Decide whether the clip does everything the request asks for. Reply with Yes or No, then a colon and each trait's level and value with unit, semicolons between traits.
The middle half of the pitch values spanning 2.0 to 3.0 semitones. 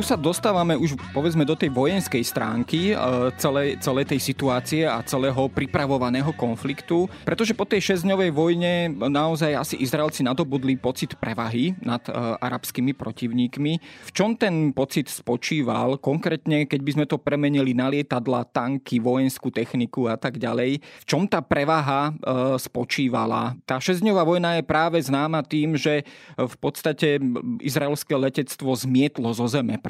No: average, 4.0 semitones